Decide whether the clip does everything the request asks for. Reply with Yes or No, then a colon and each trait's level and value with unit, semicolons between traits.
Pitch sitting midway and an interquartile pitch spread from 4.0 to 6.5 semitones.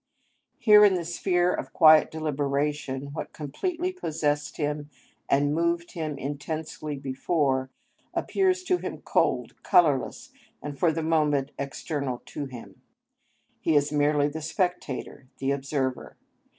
No: medium, 150 Hz; average, 3.2 semitones